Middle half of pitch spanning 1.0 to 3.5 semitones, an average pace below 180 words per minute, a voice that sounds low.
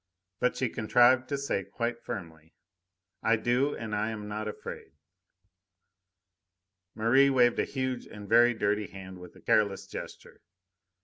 Yes: average, 3.2 semitones; average, 140 wpm; low, 115 Hz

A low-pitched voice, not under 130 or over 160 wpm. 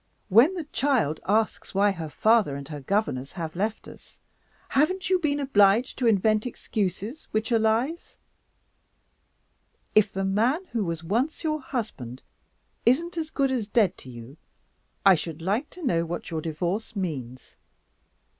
No: high, 215 Hz; average, 155 wpm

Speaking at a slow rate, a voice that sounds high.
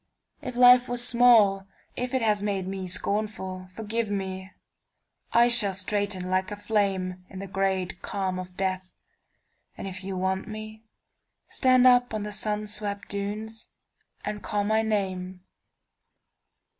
Yes: slow, 130 wpm; high, 205 Hz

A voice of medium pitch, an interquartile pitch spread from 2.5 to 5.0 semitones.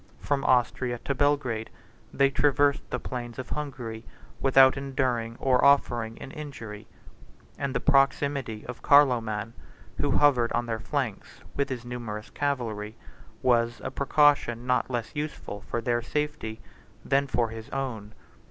No: low, 125 Hz; average, 3.4 semitones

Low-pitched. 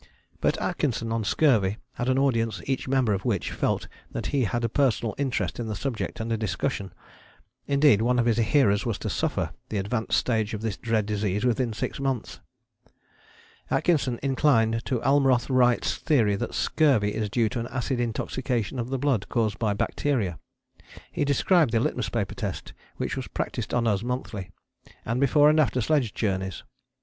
Yes: low, 115 Hz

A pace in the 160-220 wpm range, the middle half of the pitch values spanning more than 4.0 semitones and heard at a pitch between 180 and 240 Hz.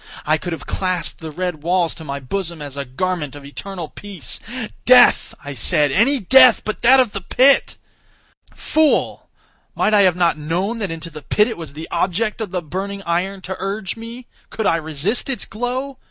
Yes: average, 195 wpm; wide, 5.4 semitones; medium, 185 Hz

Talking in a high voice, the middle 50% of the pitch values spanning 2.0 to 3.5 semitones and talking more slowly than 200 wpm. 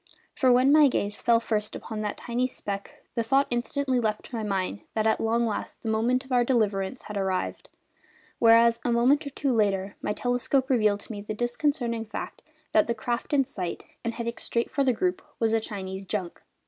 No: high, 230 Hz; average, 2.9 semitones; fast, 205 wpm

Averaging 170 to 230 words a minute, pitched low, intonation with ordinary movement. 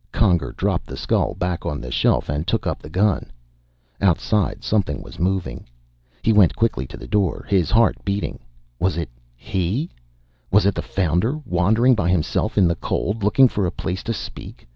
Yes: average, 185 wpm; very low, 95 Hz; average, 3.7 semitones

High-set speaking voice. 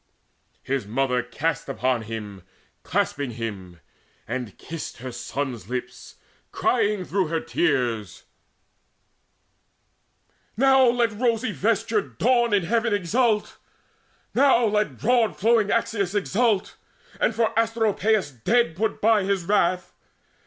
Yes: high, 200 Hz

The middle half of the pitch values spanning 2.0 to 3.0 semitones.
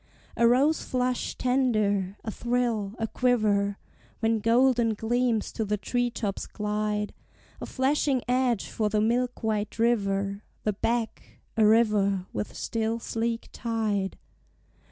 Yes: average, 2.7 semitones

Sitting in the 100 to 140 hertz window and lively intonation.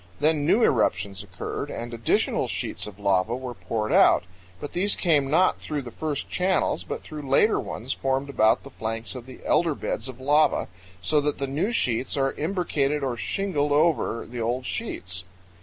No: low, 135 Hz; average, 4.7 semitones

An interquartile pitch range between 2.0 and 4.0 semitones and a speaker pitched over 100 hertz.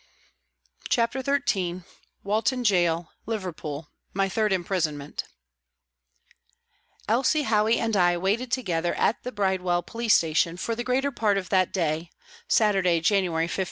No: average, 4.5 semitones; high, 190 Hz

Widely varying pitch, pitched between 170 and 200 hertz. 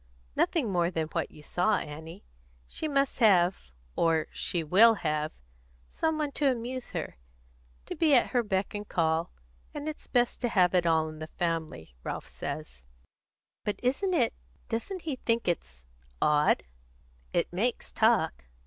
Yes: wide, 7.7 semitones; medium, 185 Hz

